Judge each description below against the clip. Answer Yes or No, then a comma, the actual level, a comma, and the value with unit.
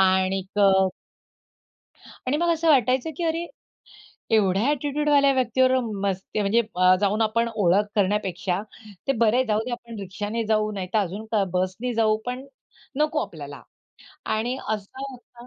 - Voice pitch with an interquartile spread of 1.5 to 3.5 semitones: No, average, 4.7 semitones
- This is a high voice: Yes, high, 220 Hz